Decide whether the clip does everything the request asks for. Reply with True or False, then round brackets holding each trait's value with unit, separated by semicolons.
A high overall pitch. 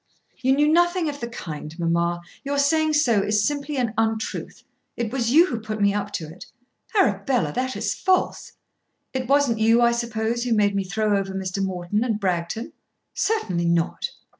True (220 Hz)